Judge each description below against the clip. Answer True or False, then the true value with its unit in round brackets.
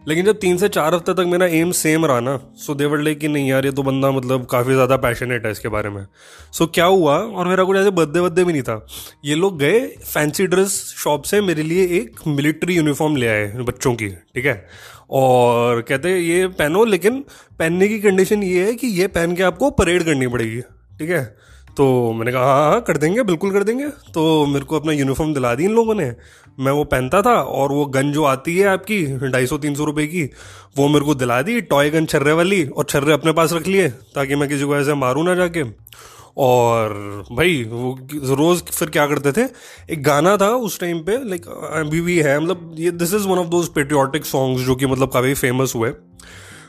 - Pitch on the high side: False (150 Hz)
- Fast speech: True (220 wpm)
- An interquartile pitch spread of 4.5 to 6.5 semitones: True (5.5 semitones)